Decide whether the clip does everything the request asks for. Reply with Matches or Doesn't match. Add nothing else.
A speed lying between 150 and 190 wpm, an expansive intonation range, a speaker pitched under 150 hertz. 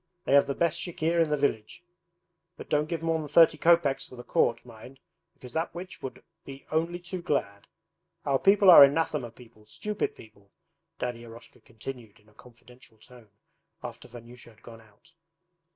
Matches